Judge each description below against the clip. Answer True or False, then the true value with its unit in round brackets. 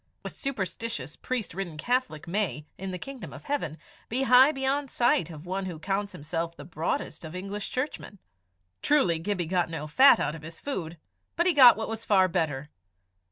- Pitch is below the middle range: False (190 Hz)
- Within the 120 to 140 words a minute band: False (185 wpm)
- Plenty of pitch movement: True (7.2 semitones)